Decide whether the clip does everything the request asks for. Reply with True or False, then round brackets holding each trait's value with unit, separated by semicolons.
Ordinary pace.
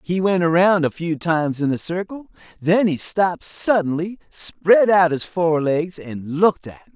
True (180 wpm)